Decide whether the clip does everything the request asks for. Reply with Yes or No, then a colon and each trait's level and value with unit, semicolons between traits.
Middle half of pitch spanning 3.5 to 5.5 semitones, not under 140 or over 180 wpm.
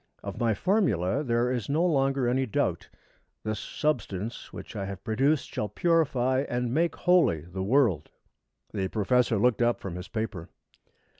Yes: average, 5.2 semitones; average, 155 wpm